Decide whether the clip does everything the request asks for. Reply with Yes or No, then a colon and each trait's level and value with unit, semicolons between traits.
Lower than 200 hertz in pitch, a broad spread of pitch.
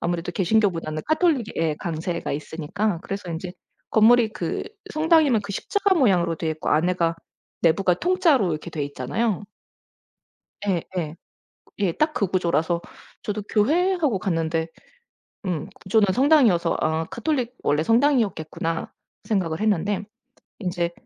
Yes: high, 190 Hz; wide, 6.0 semitones